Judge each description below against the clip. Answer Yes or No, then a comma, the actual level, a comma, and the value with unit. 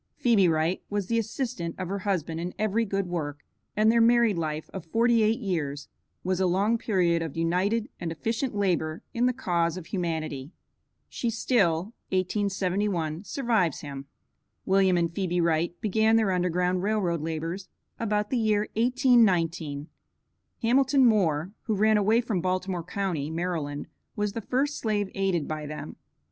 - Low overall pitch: No, medium, 185 Hz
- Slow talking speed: No, average, 155 wpm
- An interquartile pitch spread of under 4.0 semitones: No, average, 4.6 semitones